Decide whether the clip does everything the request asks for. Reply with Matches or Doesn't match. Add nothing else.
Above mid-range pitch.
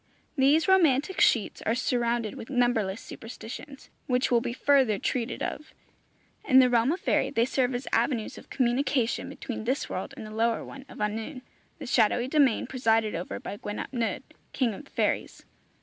Matches